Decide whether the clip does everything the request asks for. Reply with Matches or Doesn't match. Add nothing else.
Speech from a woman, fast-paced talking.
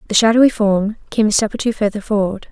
Matches